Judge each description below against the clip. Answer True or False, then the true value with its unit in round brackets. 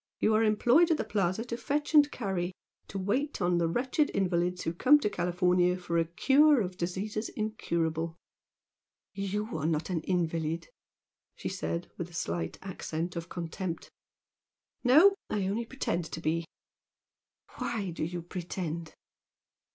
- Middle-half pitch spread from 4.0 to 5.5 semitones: True (4.5 semitones)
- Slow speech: False (150 wpm)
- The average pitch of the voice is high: False (180 Hz)